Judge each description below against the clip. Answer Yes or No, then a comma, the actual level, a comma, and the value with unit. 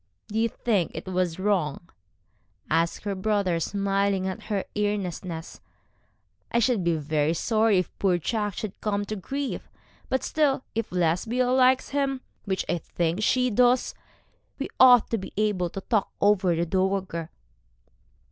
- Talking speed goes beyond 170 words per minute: No, average, 150 wpm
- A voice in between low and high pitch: No, high, 200 Hz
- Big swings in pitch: No, average, 4.1 semitones